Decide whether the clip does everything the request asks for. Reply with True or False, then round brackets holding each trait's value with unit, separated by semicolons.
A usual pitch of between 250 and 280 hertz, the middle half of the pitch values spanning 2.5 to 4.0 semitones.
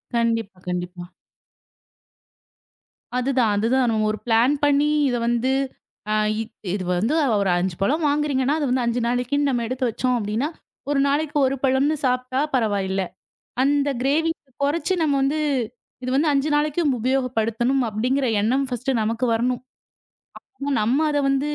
True (255 Hz; 3.7 semitones)